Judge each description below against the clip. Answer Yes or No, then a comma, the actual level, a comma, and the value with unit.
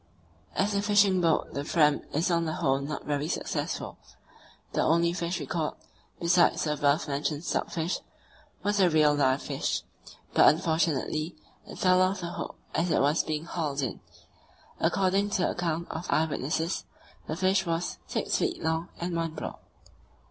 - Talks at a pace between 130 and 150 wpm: No, average, 170 wpm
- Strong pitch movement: No, average, 3.0 semitones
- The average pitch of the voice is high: No, medium, 165 Hz